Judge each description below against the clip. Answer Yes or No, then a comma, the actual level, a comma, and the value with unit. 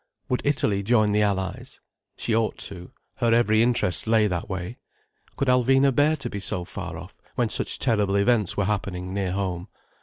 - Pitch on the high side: No, low, 105 Hz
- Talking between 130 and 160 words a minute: No, average, 180 wpm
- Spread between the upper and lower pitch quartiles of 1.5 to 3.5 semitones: No, average, 3.9 semitones